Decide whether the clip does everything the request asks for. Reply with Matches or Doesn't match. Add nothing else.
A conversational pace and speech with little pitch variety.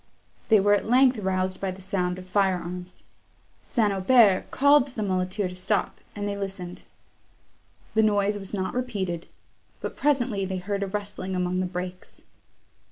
Matches